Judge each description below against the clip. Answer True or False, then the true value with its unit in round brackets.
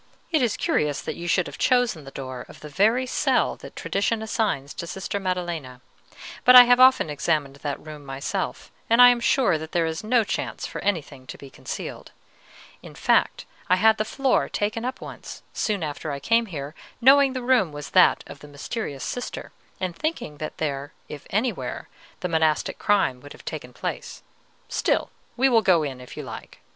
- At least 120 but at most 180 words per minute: False (195 wpm)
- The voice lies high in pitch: False (180 Hz)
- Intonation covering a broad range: True (8.1 semitones)